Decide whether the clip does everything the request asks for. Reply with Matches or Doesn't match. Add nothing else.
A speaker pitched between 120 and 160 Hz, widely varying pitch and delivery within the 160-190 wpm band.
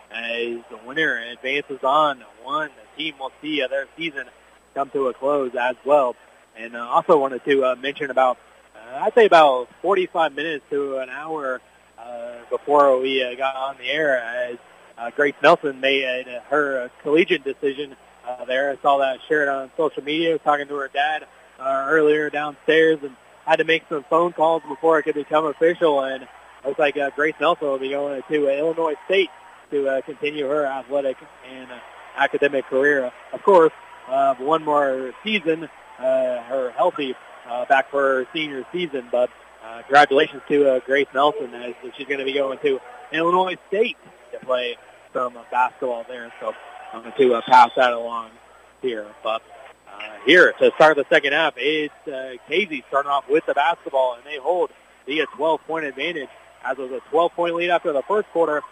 Doesn't match